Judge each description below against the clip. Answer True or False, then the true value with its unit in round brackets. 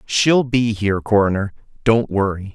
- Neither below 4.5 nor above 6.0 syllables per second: True (4.6 syllables/s)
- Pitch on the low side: True (105 Hz)